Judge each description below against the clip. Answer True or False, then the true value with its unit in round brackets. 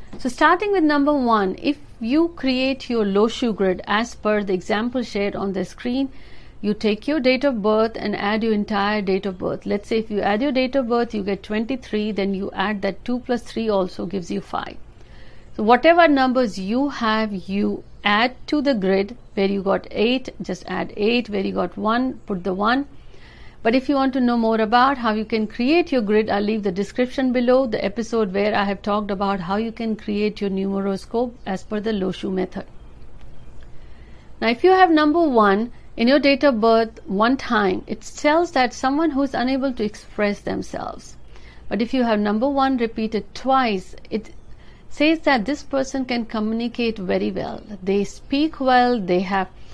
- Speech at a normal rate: False (195 wpm)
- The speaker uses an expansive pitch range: False (4.2 semitones)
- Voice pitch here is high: True (225 Hz)